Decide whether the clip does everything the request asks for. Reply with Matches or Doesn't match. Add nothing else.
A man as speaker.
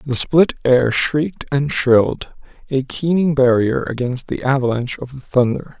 Matches